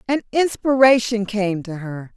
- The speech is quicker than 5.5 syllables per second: No, 4.2 syllables/s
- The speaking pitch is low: No, high, 220 Hz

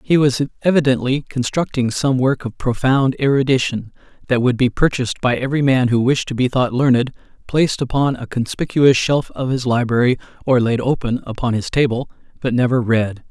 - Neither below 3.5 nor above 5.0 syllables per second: No, 5.4 syllables/s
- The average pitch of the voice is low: Yes, low, 130 Hz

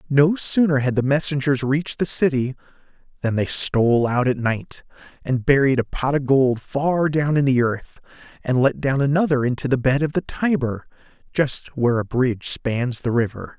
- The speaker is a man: Yes, male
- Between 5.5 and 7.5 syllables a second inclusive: No, 4.9 syllables/s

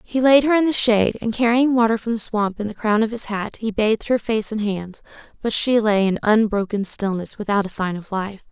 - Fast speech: Yes, fast, 245 wpm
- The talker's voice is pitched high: Yes, high, 215 Hz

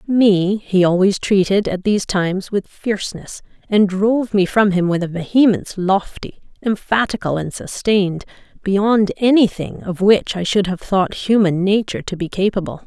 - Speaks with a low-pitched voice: No, high, 195 Hz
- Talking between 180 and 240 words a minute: No, average, 165 wpm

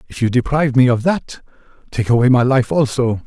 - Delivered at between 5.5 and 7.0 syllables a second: Yes, 5.8 syllables/s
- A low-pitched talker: Yes, low, 130 Hz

